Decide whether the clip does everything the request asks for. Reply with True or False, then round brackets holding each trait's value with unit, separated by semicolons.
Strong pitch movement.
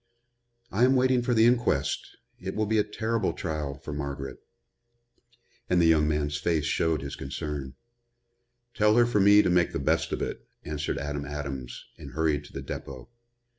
True (6.4 semitones)